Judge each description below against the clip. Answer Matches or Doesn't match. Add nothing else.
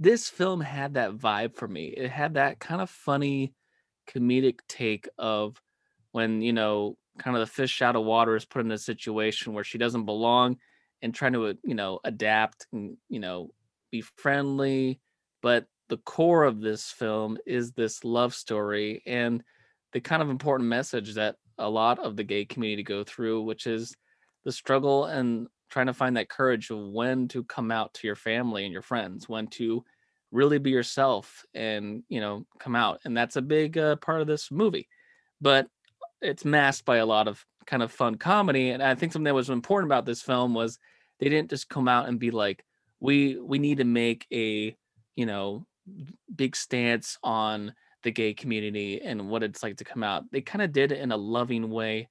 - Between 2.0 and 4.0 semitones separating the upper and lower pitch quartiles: Matches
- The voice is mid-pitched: Doesn't match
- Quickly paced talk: Doesn't match